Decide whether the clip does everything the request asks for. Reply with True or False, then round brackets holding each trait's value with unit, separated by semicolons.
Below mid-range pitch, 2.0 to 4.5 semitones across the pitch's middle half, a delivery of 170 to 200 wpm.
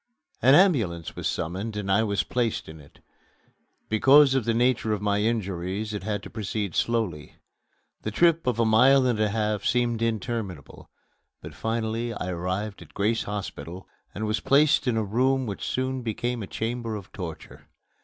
True (110 Hz; 3.2 semitones; 175 wpm)